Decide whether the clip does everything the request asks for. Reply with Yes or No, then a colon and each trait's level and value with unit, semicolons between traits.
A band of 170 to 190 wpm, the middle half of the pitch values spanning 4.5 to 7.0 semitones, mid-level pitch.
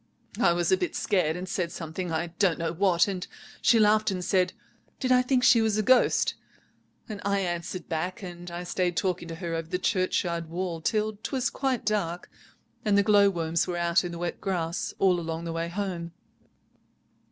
No: average, 185 wpm; average, 3.0 semitones; medium, 180 Hz